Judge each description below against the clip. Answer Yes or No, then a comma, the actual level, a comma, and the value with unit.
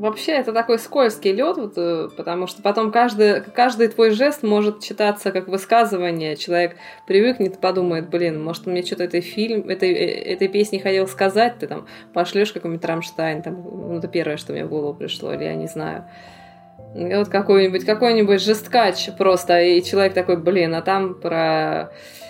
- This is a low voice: No, high, 190 Hz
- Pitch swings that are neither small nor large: Yes, average, 3.7 semitones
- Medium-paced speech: No, fast, 165 wpm